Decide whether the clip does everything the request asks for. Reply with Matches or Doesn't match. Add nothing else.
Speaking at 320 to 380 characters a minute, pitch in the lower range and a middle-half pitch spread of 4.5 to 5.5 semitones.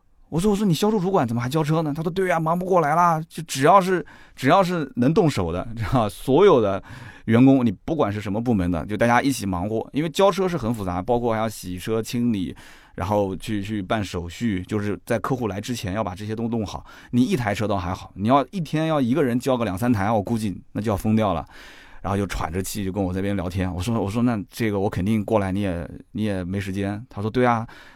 Matches